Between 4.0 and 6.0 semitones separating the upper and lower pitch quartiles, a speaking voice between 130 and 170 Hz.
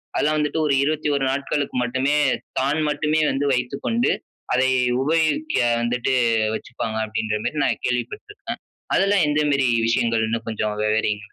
Yes: average, 4.8 semitones; low, 135 Hz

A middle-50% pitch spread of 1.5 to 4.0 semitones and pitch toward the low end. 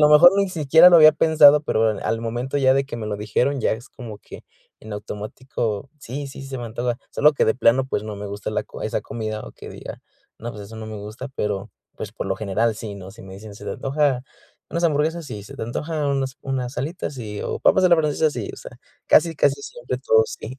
No: average, 5.1 semitones; low, 125 Hz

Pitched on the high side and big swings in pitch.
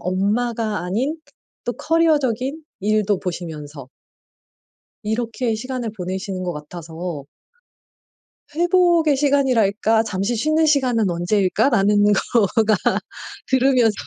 Yes: high, 220 Hz; wide, 5.8 semitones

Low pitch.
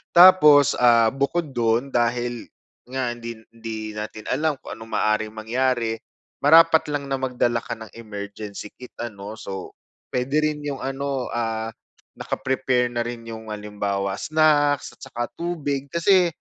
Yes: low, 120 Hz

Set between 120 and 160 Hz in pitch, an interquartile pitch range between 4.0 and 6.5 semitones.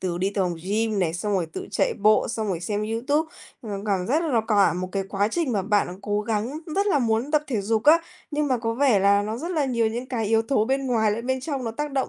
No: high, 225 Hz; average, 4.5 semitones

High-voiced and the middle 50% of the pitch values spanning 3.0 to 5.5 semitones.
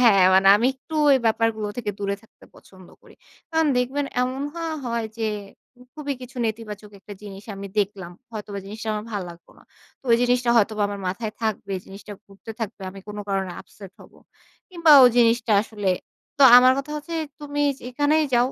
Yes: high, 220 Hz; average, 3.9 semitones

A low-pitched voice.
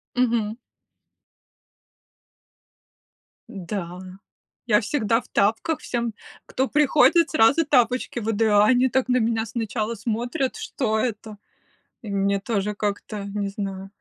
No: high, 225 Hz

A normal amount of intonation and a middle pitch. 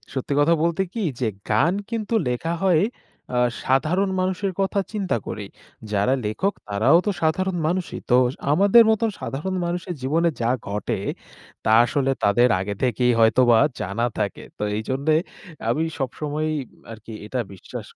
No: wide, 7.8 semitones; medium, 145 Hz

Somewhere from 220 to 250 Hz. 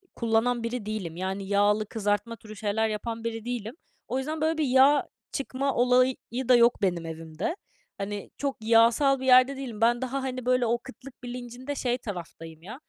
Yes: high, 235 Hz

